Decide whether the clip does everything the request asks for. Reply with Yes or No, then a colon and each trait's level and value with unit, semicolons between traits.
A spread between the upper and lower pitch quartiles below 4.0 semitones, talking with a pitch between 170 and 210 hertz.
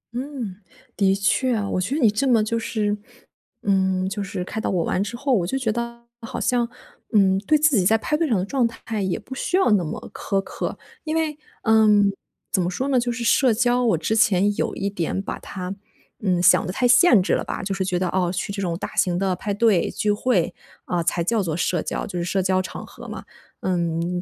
No: average, 4.3 semitones; high, 205 Hz